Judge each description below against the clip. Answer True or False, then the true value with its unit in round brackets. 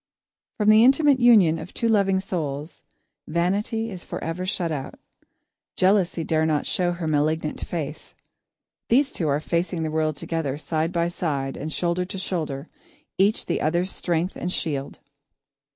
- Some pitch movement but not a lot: True (3.5 semitones)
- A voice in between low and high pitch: True (170 Hz)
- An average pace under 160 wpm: True (150 wpm)